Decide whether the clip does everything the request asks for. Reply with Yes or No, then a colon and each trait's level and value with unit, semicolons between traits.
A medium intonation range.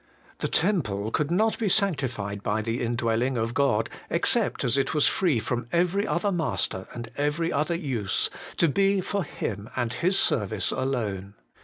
No: wide, 7.3 semitones